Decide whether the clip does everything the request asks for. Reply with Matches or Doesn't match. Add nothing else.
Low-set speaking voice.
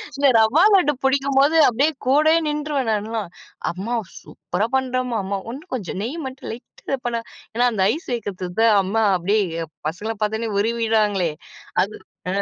Doesn't match